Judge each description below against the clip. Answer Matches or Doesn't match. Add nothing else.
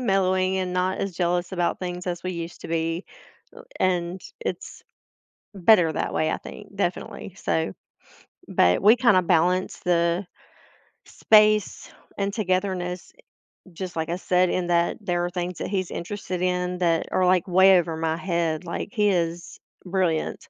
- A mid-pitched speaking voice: Matches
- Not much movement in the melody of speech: Matches